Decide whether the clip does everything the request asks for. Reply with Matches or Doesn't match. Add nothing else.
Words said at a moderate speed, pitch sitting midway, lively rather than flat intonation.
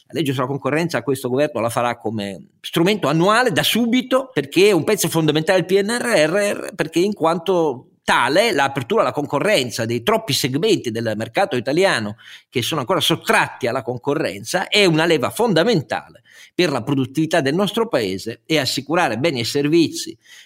Matches